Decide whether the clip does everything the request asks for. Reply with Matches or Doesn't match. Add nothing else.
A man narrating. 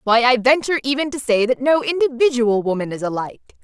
Doesn't match